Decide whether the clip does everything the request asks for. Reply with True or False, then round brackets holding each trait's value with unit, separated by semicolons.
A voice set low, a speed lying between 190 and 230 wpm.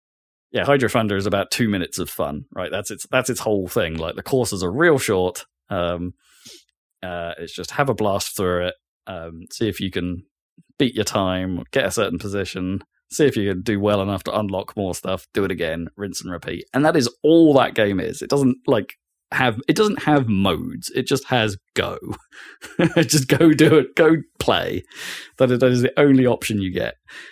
True (105 Hz; 200 wpm)